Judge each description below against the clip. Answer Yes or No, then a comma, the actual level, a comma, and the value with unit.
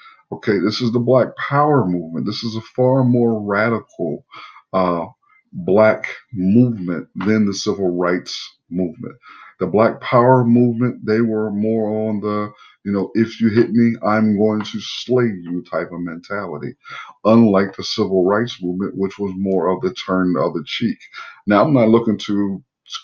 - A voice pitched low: Yes, low, 105 Hz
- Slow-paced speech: No, average, 165 wpm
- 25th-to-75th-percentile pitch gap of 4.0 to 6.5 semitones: No, average, 3.5 semitones